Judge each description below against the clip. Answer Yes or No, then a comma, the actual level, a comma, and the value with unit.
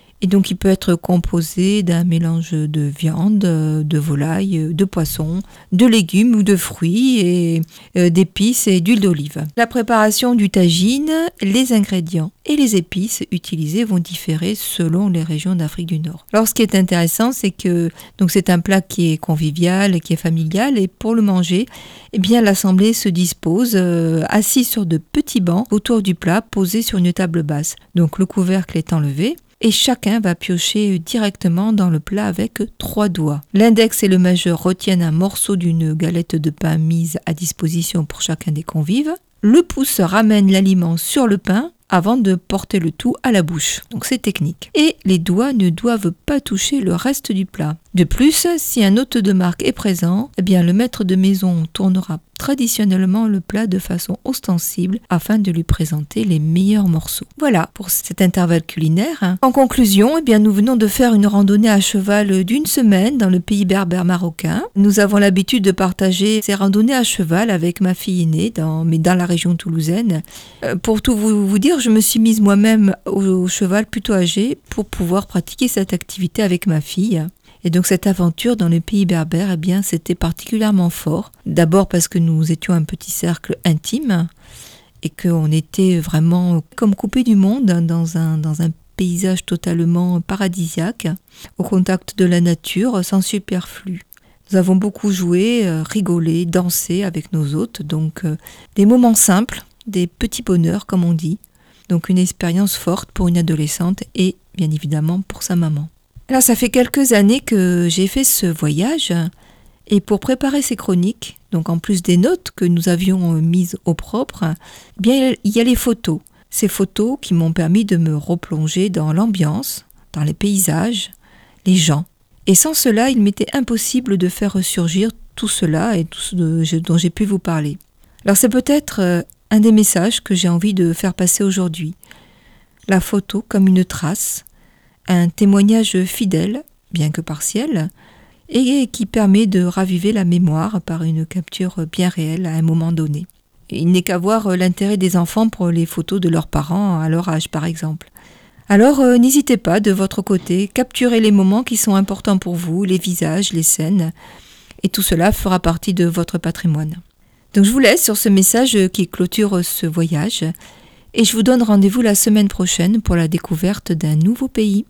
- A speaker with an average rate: Yes, average, 180 wpm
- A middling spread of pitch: Yes, average, 3.8 semitones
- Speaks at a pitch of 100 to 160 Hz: No, medium, 185 Hz